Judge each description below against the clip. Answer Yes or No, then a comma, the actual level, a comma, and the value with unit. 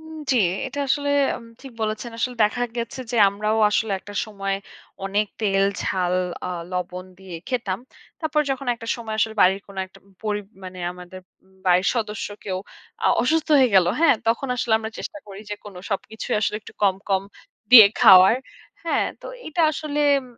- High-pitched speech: Yes, high, 215 Hz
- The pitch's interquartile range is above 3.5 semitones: Yes, average, 4.3 semitones